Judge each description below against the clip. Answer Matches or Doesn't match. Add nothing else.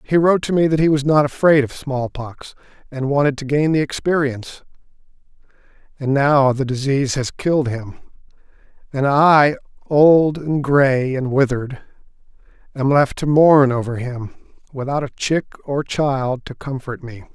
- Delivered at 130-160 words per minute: Matches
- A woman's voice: Doesn't match